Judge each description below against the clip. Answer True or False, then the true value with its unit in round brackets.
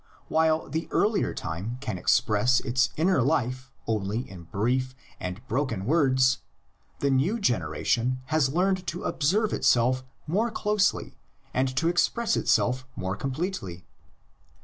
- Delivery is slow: True (130 wpm)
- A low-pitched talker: True (130 Hz)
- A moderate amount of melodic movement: False (5.9 semitones)